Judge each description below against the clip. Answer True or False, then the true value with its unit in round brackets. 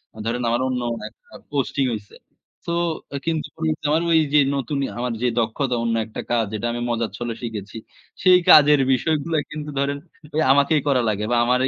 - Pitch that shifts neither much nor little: True (4.2 semitones)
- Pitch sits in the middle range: False (125 Hz)